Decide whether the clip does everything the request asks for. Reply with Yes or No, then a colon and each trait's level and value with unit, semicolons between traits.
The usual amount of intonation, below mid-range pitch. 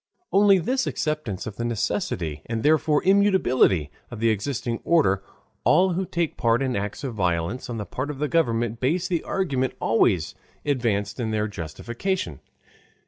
No: wide, 7.4 semitones; low, 120 Hz